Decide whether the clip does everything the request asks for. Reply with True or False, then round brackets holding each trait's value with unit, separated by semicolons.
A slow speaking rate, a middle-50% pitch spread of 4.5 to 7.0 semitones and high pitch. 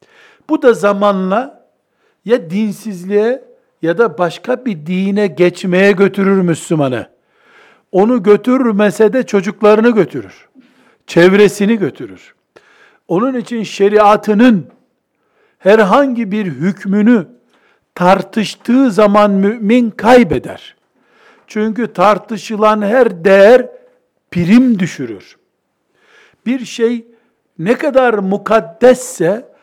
False (85 wpm; 3.6 semitones; 215 Hz)